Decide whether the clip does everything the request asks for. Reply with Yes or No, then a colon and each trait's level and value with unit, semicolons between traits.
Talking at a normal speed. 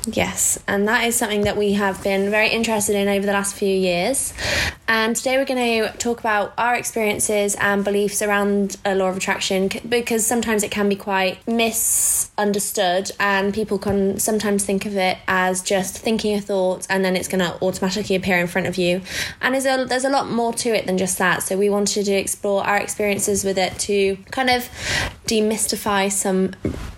Yes: average, 195 wpm